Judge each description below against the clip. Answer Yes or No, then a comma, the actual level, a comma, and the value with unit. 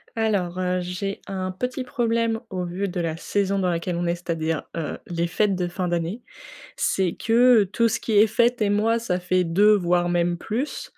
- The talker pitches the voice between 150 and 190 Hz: Yes, medium, 185 Hz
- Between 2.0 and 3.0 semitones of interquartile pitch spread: No, average, 3.6 semitones